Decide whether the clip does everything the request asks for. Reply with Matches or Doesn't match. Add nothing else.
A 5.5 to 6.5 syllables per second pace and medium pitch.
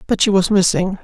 Doesn't match